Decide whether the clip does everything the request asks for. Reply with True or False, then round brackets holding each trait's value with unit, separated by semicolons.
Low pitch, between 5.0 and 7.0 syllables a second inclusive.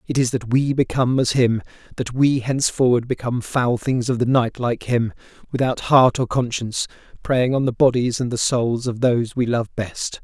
True (125 Hz; 5.1 syllables/s)